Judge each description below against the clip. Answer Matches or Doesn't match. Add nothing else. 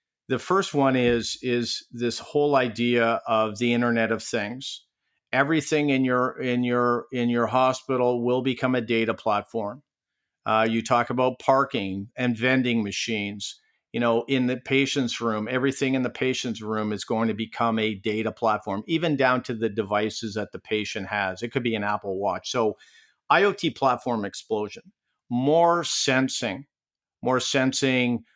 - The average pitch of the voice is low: Matches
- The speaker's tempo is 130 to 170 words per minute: Matches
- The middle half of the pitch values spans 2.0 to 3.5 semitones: Matches